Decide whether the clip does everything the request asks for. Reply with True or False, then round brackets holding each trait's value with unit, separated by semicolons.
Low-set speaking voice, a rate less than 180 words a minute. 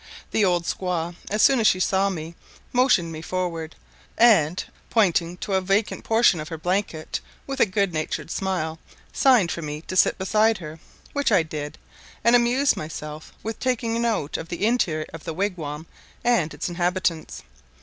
False (185 Hz; 170 wpm)